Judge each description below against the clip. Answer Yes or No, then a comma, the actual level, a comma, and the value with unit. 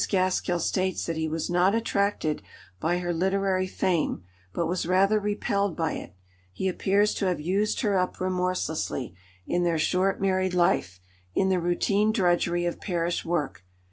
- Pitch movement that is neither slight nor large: No, narrow, 2.2 semitones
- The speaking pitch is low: No, medium, 180 Hz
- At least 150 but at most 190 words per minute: Yes, average, 160 wpm